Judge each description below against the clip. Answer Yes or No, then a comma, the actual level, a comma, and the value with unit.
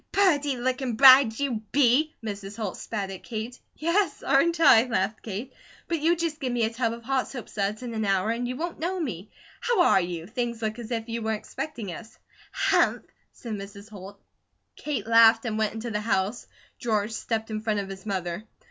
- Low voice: No, high, 225 Hz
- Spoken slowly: No, average, 200 wpm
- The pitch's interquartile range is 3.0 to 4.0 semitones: Yes, average, 3.7 semitones